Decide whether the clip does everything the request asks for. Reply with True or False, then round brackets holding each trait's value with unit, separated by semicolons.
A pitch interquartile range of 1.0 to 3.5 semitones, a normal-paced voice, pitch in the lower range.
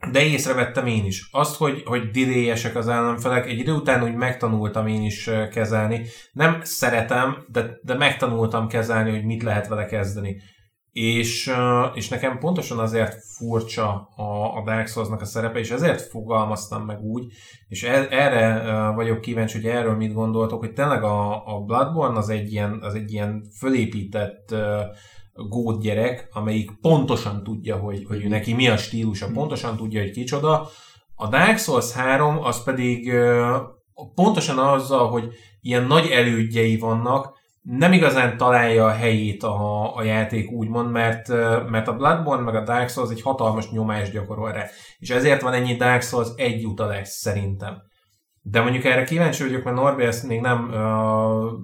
False (2.4 semitones; 160 wpm; 115 Hz)